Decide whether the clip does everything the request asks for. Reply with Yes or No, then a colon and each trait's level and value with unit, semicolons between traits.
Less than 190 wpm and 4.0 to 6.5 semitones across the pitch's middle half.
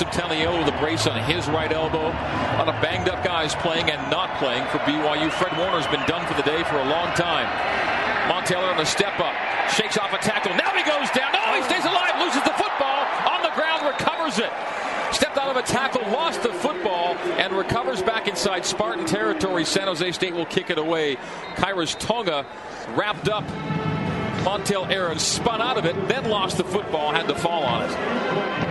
No: average, 200 wpm; average, 4.8 semitones